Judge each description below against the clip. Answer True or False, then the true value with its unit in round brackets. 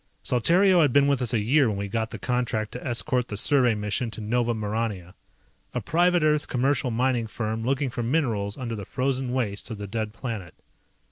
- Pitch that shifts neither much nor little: True (3.5 semitones)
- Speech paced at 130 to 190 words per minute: False (200 wpm)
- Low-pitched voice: True (120 Hz)